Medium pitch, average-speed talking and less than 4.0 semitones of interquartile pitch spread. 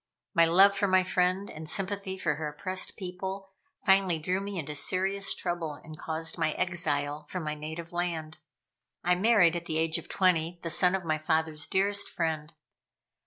Yes: medium, 175 Hz; average, 175 wpm; average, 3.1 semitones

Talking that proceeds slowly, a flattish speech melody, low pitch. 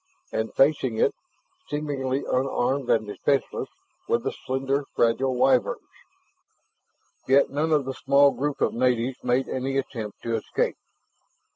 Yes: slow, 130 wpm; narrow, 2.1 semitones; low, 130 Hz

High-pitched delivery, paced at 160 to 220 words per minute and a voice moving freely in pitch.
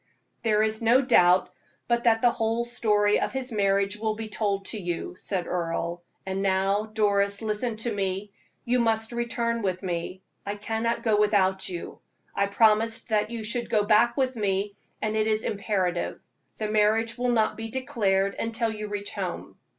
No: high, 215 Hz; average, 175 wpm; narrow, 2.4 semitones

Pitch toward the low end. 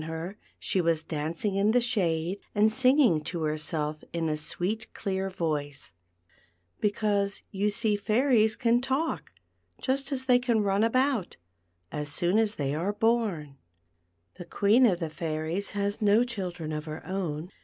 No: high, 195 Hz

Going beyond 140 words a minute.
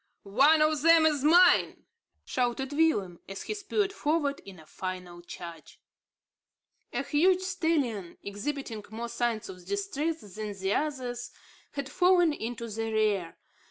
No: slow, 135 wpm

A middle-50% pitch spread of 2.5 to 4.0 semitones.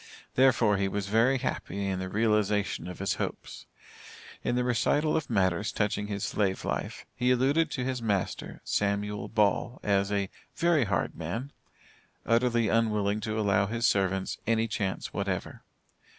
Yes: average, 3.3 semitones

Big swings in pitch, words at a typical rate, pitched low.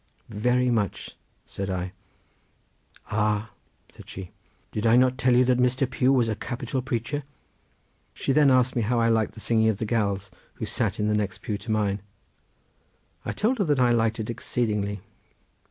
No: average, 3.1 semitones; average, 180 wpm; low, 115 Hz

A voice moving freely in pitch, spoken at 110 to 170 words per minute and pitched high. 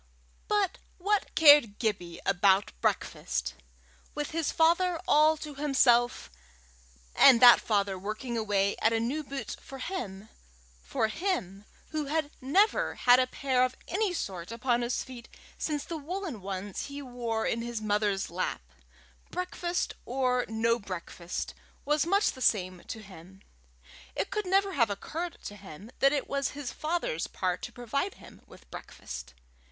Yes: wide, 7.0 semitones; average, 150 wpm; high, 245 Hz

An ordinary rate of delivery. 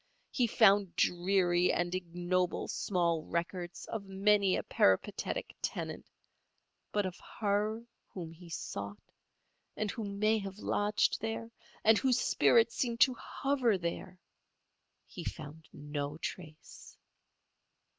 No: slow, 115 wpm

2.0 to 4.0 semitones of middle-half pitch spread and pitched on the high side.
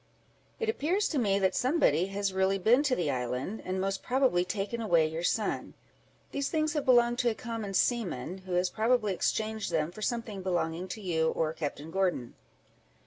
No: average, 5.3 semitones; high, 195 Hz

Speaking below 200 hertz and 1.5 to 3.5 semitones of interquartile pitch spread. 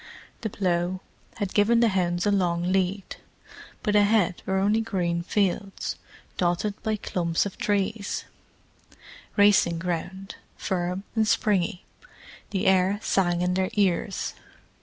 Yes: high, 190 Hz; narrow, 2.6 semitones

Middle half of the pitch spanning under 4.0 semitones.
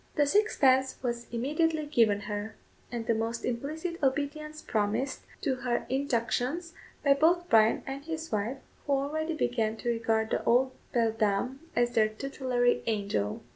No: average, 4.4 semitones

